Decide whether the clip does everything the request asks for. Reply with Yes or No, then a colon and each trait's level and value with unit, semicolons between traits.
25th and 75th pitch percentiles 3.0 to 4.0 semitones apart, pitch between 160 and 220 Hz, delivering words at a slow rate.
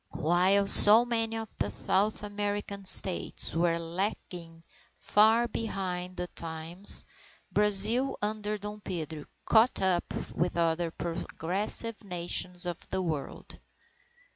Yes: average, 3.5 semitones; high, 190 Hz; slow, 115 wpm